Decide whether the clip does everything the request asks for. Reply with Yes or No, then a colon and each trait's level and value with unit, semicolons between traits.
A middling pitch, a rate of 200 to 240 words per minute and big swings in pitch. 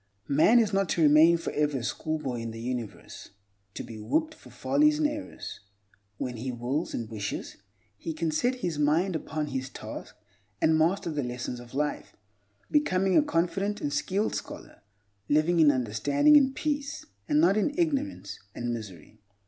No: medium, 155 Hz; average, 165 wpm; wide, 8.3 semitones